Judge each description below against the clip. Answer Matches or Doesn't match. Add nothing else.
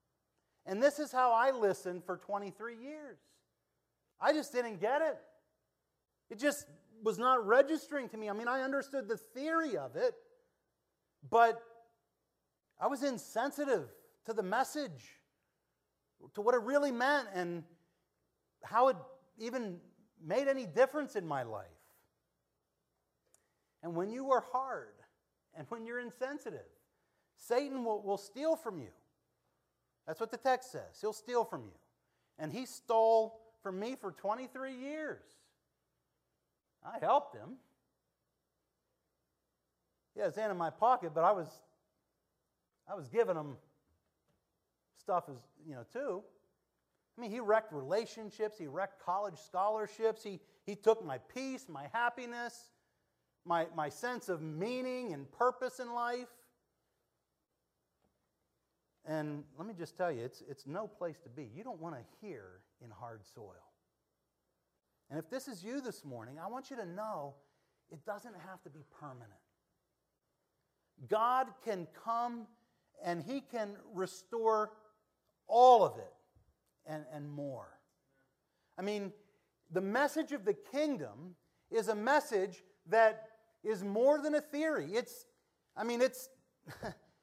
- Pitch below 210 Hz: Doesn't match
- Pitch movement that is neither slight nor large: Doesn't match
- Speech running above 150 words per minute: Doesn't match